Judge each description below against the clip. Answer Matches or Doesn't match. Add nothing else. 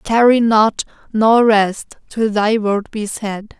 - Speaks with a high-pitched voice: Matches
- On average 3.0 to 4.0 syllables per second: Matches